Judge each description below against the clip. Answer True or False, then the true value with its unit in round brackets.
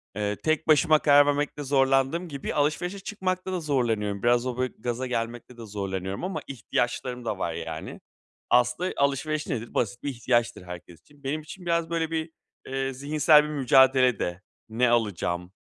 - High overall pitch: False (130 Hz)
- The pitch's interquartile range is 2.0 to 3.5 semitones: False (4.8 semitones)